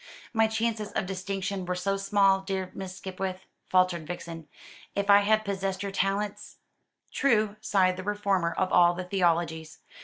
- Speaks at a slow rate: No, average, 155 wpm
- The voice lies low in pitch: No, high, 195 Hz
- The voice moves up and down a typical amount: No, narrow, 1.7 semitones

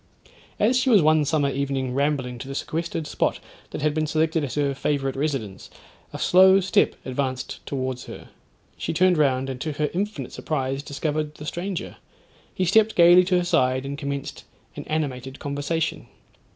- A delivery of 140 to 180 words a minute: Yes, average, 170 wpm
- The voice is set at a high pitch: No, medium, 145 Hz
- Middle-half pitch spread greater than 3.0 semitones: Yes, average, 3.5 semitones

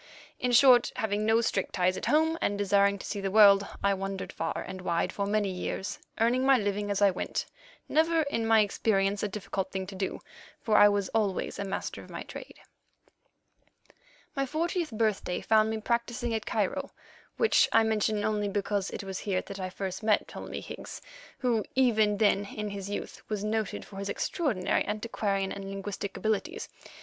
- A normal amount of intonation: No, narrow, 2.3 semitones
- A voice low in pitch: No, high, 205 Hz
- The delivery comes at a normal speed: Yes, average, 185 wpm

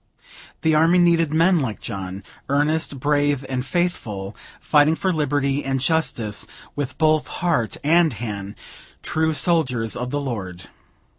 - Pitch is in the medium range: Yes, medium, 145 Hz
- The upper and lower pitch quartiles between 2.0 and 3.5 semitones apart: No, average, 5.3 semitones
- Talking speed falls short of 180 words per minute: Yes, slow, 135 wpm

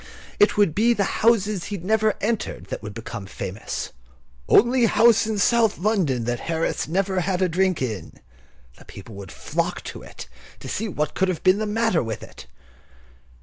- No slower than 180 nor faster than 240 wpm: Yes, average, 190 wpm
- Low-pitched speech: No, high, 190 Hz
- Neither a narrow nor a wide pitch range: No, wide, 6.3 semitones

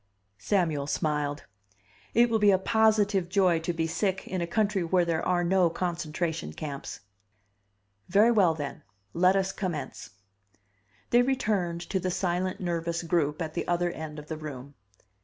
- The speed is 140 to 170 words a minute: Yes, average, 160 wpm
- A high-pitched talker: No, medium, 175 Hz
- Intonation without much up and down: No, average, 3.2 semitones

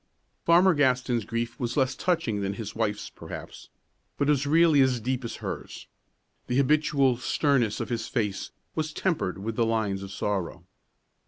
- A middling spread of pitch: Yes, average, 4.8 semitones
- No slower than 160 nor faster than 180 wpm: Yes, average, 165 wpm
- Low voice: Yes, low, 125 Hz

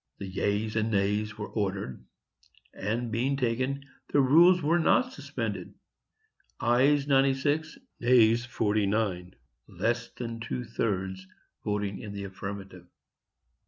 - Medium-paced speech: No, slow, 105 wpm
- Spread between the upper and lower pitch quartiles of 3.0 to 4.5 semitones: No, average, 4.9 semitones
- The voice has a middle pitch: No, low, 115 Hz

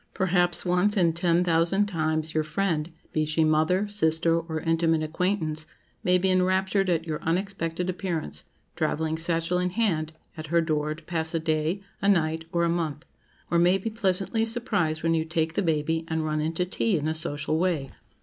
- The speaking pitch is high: No, medium, 165 Hz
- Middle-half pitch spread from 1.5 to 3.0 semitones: Yes, narrow, 2.6 semitones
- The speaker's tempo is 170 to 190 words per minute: Yes, average, 180 wpm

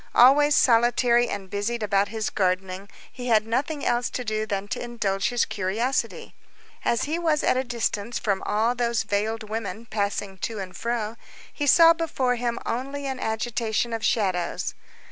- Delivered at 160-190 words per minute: Yes, average, 165 wpm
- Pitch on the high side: Yes, high, 230 Hz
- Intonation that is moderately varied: Yes, average, 3.2 semitones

